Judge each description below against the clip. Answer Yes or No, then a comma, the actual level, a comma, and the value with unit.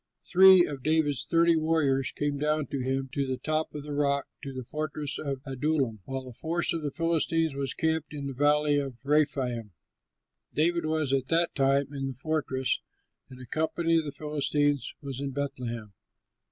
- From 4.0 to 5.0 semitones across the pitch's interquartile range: No, narrow, 2.6 semitones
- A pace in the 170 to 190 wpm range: Yes, average, 180 wpm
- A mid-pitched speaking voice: Yes, medium, 145 Hz